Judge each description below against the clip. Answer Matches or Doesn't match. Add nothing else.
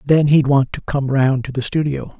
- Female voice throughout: Doesn't match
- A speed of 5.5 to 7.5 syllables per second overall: Doesn't match